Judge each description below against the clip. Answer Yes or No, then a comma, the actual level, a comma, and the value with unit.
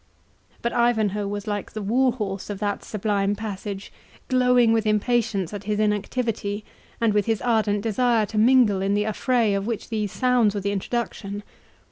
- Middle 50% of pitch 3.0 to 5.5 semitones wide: No, narrow, 2.4 semitones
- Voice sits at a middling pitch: No, high, 210 Hz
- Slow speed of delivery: No, average, 170 wpm